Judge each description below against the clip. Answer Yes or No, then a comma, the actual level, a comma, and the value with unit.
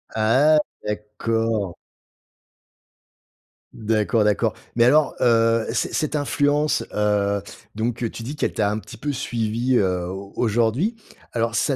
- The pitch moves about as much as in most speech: Yes, average, 3.3 semitones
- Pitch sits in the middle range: No, low, 115 Hz